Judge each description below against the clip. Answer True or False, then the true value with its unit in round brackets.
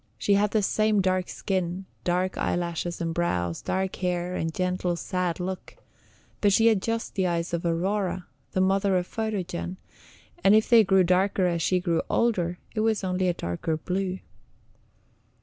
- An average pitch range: False (2.1 semitones)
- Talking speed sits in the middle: True (165 wpm)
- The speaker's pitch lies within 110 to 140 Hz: False (185 Hz)